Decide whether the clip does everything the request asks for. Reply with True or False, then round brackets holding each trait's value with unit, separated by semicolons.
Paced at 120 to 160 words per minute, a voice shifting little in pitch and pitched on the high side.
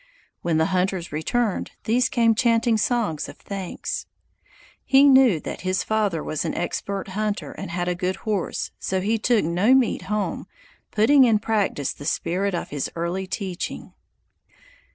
False (155 wpm; 4.2 semitones; 195 Hz)